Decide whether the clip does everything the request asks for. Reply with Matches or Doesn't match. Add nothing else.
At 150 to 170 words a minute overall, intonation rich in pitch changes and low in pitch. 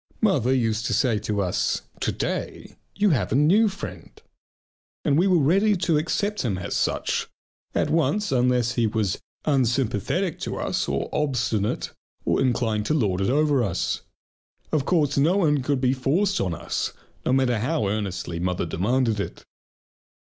Matches